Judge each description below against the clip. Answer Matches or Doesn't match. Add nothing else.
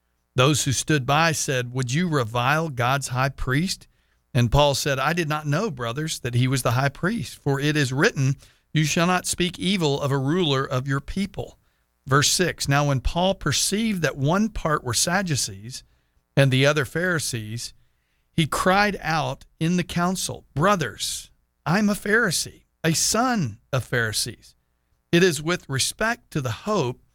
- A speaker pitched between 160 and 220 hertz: Doesn't match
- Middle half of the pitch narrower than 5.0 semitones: Doesn't match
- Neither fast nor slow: Matches